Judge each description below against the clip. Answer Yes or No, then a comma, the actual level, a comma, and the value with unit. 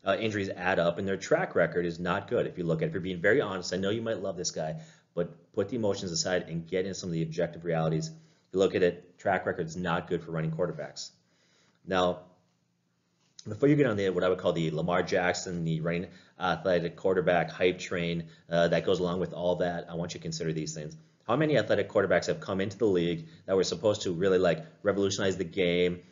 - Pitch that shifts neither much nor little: No, narrow, 1.8 semitones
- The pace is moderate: No, fast, 240 wpm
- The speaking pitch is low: Yes, very low, 90 Hz